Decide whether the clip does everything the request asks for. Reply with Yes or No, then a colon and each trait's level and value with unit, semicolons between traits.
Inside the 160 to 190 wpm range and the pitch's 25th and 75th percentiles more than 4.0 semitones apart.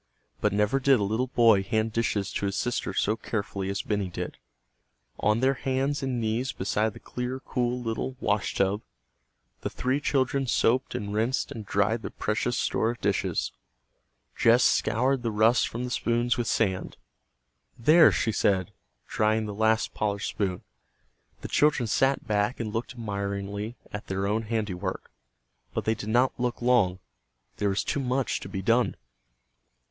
No: average, 165 wpm; average, 3.3 semitones